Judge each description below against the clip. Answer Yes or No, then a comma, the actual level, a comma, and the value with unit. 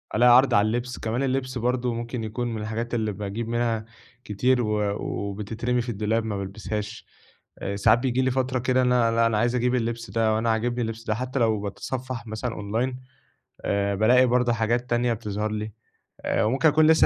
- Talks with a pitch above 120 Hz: No, low, 115 Hz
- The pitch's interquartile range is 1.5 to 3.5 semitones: Yes, narrow, 2.4 semitones